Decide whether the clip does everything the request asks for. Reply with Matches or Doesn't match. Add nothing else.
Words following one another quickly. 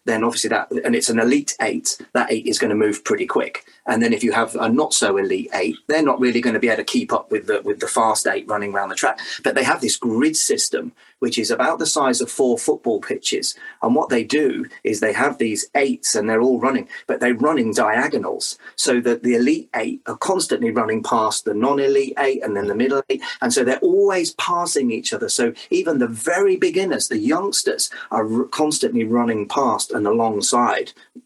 Matches